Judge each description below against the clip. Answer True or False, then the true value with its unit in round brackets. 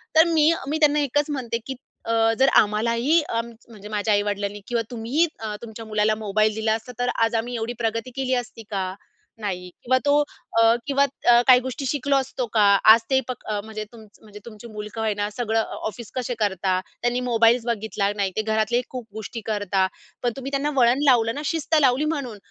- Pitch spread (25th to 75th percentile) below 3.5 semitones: True (3.1 semitones)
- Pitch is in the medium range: False (230 Hz)